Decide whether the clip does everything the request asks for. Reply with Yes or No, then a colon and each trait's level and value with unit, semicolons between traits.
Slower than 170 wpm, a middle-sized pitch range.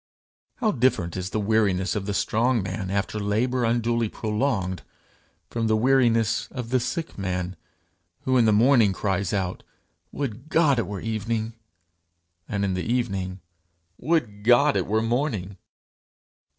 Yes: average, 145 wpm; average, 3.8 semitones